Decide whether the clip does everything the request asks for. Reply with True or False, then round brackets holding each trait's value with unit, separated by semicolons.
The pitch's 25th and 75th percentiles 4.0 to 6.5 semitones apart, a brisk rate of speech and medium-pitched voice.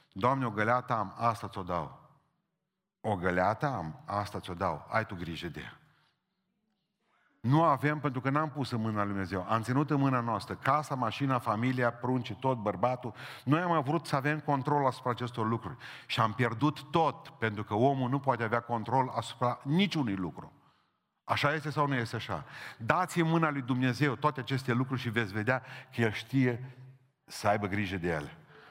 False (4.7 semitones; 180 wpm; 125 Hz)